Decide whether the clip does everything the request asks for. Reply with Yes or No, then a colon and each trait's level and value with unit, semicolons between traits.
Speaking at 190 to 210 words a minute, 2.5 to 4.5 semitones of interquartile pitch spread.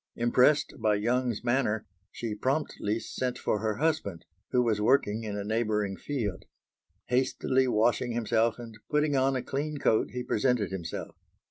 No: average, 150 wpm; average, 3.5 semitones